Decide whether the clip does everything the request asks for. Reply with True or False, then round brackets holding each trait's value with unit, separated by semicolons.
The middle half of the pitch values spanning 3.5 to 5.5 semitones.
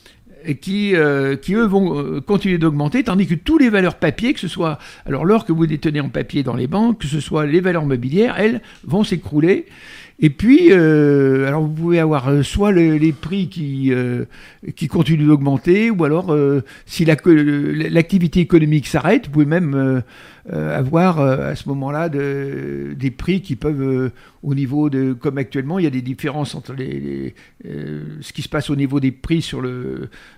True (4.2 semitones)